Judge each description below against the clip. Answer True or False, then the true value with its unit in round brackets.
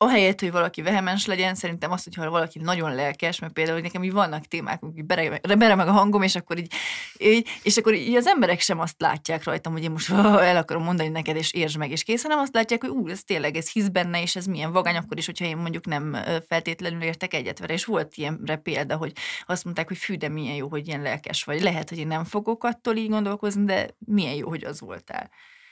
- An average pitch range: True (4.0 semitones)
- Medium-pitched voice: True (175 Hz)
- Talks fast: True (235 wpm)